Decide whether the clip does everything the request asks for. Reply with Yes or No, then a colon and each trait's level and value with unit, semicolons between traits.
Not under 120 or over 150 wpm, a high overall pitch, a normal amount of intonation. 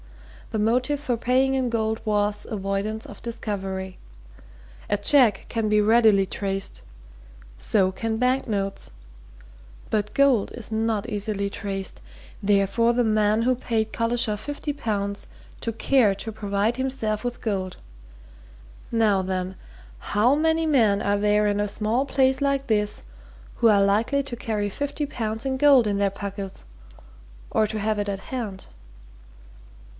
Yes: average, 140 wpm; high, 215 Hz; average, 3.2 semitones